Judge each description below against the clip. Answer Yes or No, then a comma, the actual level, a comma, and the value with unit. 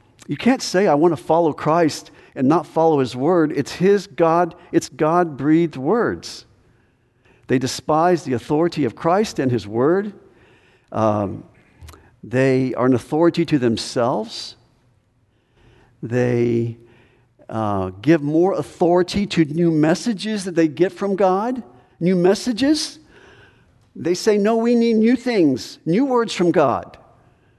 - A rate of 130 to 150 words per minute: Yes, slow, 135 wpm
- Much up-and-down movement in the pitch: Yes, wide, 6.8 semitones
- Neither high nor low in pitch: Yes, medium, 160 Hz